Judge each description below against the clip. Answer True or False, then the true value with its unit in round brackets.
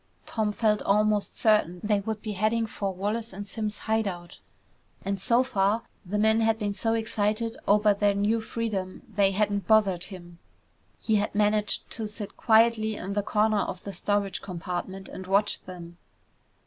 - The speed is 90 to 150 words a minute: False (170 wpm)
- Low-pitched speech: False (210 Hz)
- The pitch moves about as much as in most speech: False (2.0 semitones)